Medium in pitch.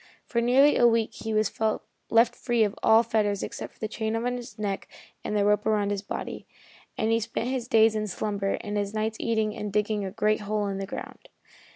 No: high, 215 Hz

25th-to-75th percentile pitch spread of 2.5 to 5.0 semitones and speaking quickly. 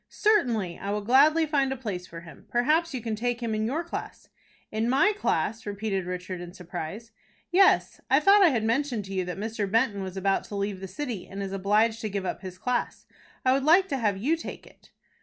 No: wide, 5.6 semitones; fast, 225 wpm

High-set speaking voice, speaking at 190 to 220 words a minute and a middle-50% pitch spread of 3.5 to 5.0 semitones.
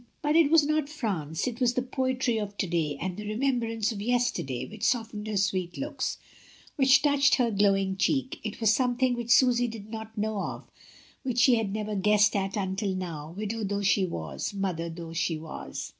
Yes: high, 215 Hz; average, 200 wpm; average, 4.4 semitones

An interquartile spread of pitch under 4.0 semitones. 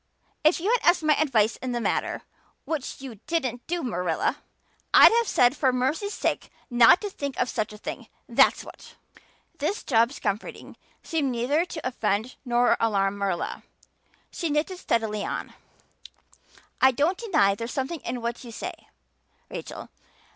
No: wide, 5.6 semitones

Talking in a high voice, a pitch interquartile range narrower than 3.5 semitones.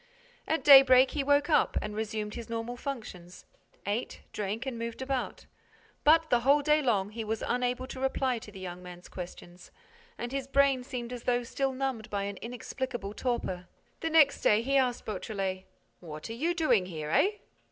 No: high, 240 Hz; average, 4.6 semitones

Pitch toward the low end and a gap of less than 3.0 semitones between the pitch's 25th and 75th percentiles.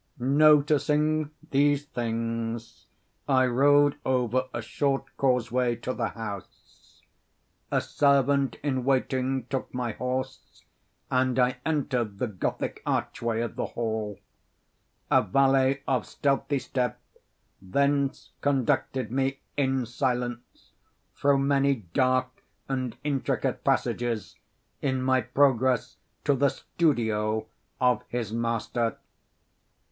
Yes: low, 130 Hz; narrow, 2.6 semitones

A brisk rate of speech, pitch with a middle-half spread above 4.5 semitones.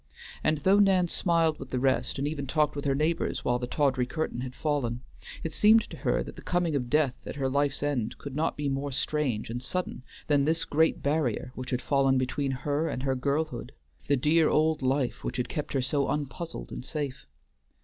No: fast, 210 wpm; average, 3.1 semitones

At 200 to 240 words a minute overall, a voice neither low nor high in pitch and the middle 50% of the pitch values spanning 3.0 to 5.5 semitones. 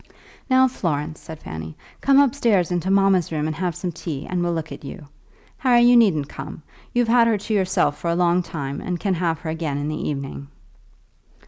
Yes: fast, 205 wpm; medium, 175 Hz; average, 4.9 semitones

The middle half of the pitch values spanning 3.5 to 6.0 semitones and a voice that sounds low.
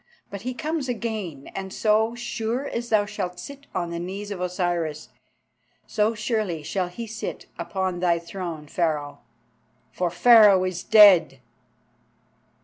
No: average, 4.2 semitones; high, 195 Hz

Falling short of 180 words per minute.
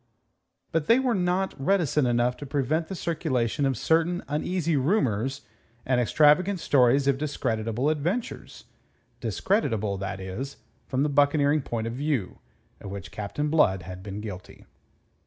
Yes: average, 140 wpm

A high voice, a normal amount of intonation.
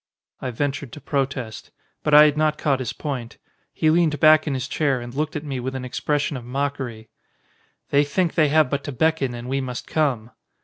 No: medium, 140 Hz; average, 3.0 semitones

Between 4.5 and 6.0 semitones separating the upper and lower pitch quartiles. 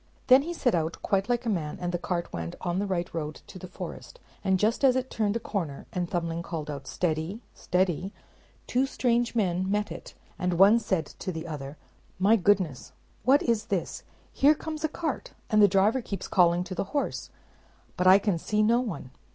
Yes: average, 5.1 semitones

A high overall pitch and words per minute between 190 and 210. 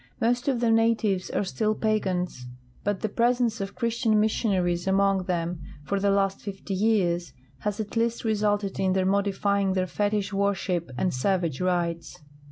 No: high, 200 Hz; average, 165 wpm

